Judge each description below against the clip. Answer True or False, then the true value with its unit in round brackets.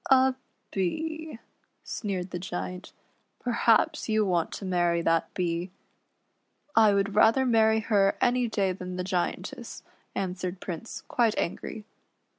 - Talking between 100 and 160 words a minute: True (140 wpm)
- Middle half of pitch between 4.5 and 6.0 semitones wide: False (4.0 semitones)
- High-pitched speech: True (195 Hz)